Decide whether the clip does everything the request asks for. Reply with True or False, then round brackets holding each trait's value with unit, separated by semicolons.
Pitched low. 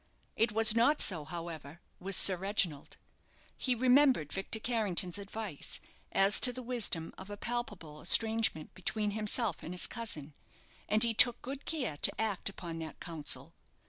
False (205 Hz)